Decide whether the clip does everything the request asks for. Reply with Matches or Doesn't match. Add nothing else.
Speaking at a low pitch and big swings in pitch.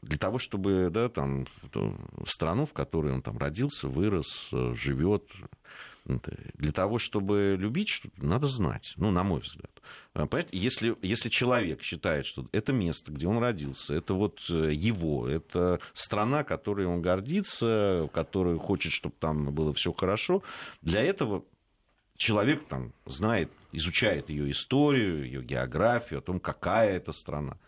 Matches